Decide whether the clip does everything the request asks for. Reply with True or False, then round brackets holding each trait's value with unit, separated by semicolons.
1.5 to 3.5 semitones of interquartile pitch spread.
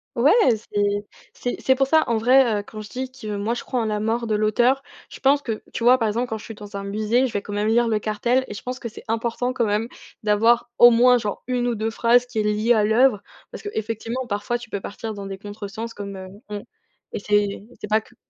True (2.6 semitones)